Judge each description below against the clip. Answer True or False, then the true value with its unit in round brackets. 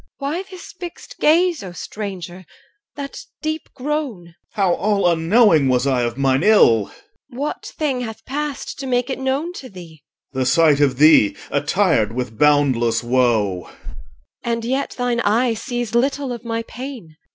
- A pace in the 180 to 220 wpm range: False (170 wpm)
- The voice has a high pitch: True (210 Hz)